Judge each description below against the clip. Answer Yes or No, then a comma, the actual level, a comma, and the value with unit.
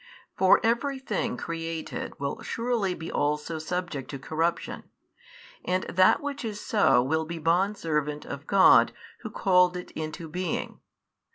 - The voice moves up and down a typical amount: Yes, average, 3.9 semitones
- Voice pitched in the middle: Yes, medium, 175 Hz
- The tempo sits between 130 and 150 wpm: Yes, average, 140 wpm